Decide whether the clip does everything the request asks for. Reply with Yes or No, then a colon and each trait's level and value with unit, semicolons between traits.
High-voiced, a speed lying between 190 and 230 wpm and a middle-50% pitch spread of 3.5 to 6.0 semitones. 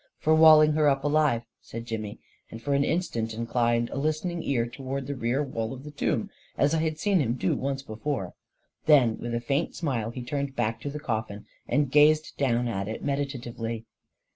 No: low, 135 Hz; average, 200 wpm; average, 4.2 semitones